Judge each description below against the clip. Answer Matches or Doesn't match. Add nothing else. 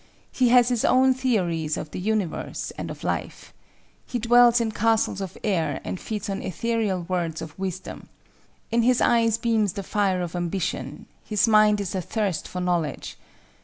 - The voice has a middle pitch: Doesn't match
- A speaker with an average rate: Matches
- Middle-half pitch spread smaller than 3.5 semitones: Doesn't match